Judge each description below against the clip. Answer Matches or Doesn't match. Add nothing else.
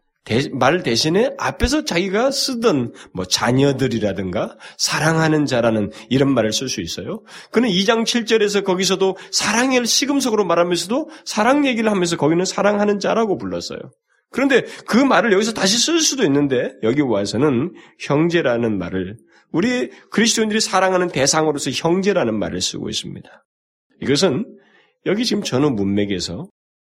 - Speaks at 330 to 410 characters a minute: Matches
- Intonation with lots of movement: Matches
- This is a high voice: Doesn't match